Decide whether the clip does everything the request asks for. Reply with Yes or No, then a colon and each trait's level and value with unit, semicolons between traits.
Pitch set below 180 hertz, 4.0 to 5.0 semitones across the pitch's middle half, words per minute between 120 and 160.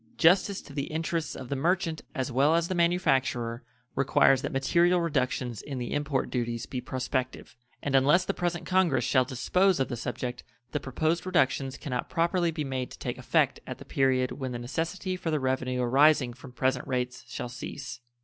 No: low, 135 Hz; average, 4.7 semitones; average, 190 wpm